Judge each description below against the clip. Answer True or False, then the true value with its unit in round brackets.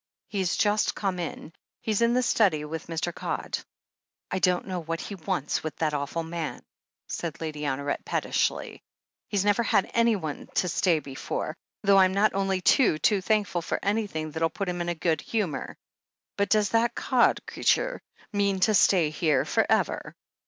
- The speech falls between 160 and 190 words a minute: True (175 wpm)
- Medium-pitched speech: True (180 Hz)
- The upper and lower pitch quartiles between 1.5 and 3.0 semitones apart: False (4.2 semitones)